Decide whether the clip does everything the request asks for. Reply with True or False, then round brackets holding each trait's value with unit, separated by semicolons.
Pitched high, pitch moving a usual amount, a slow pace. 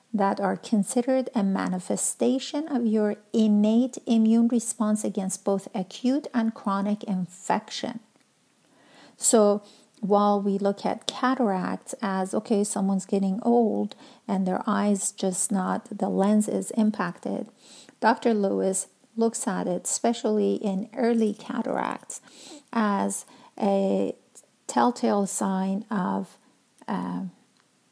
True (215 Hz; 3.5 semitones; 110 wpm)